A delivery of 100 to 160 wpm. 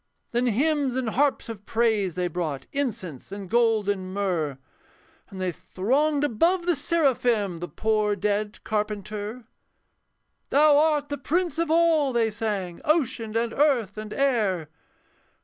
Yes: average, 140 wpm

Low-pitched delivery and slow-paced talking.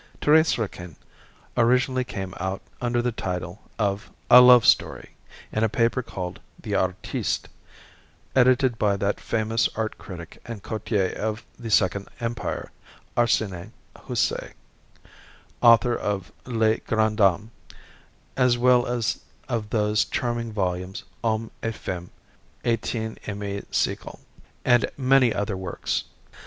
Yes: low, 110 Hz; slow, 120 wpm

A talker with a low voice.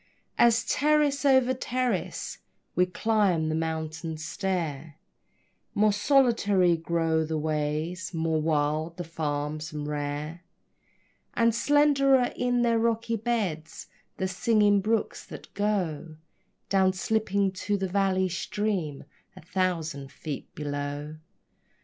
No: medium, 180 Hz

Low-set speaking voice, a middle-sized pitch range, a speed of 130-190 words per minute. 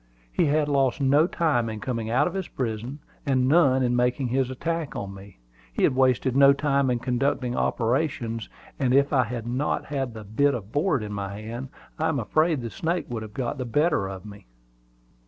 No: low, 130 Hz; average, 3.7 semitones; fast, 205 wpm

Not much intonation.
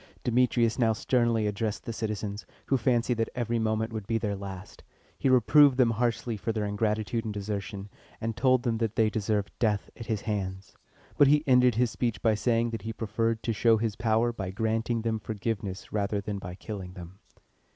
Yes: narrow, 2.2 semitones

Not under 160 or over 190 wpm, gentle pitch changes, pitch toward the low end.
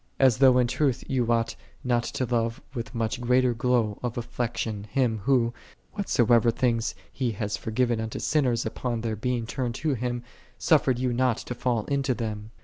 Yes: average, 180 wpm; narrow, 1.8 semitones; low, 120 Hz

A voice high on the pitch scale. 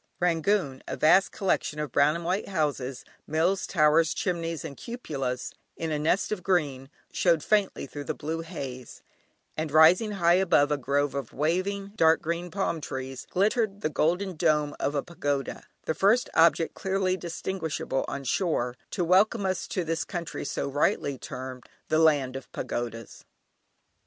No: medium, 160 Hz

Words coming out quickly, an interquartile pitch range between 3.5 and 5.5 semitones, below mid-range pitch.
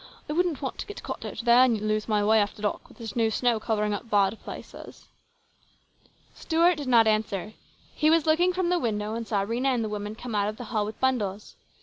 No: fast, 230 wpm; average, 3.8 semitones; high, 225 Hz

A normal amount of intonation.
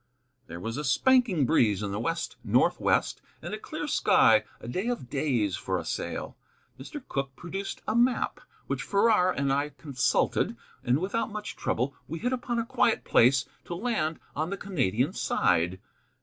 No: wide, 9.0 semitones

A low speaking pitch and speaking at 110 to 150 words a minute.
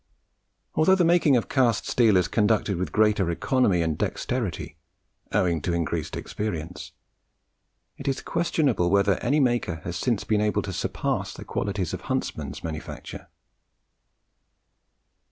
Yes: low, 105 Hz; slow, 135 wpm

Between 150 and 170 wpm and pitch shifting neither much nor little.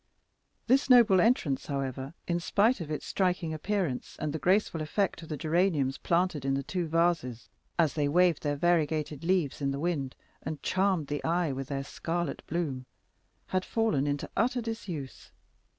Yes: average, 165 wpm; average, 4.4 semitones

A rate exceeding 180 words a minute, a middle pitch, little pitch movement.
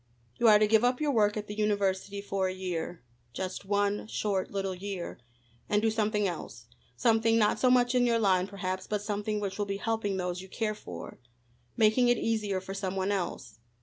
No: fast, 205 wpm; high, 205 Hz; narrow, 2.3 semitones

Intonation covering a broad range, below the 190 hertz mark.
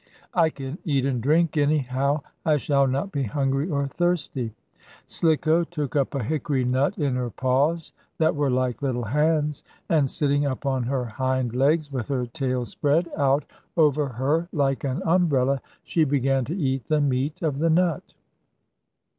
No: average, 2.9 semitones; medium, 140 Hz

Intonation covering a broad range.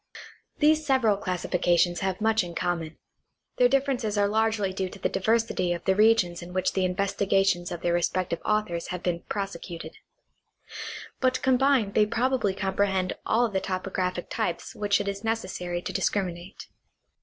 No: average, 3.6 semitones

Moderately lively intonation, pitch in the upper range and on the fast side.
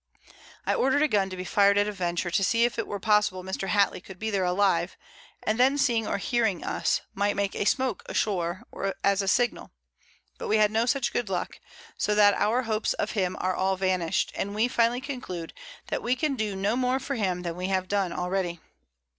Yes: average, 3.8 semitones; high, 205 Hz; fast, 220 wpm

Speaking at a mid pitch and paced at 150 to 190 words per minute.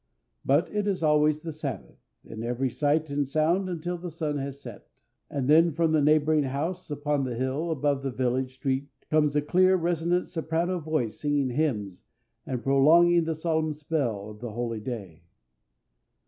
Yes: medium, 150 Hz; average, 170 wpm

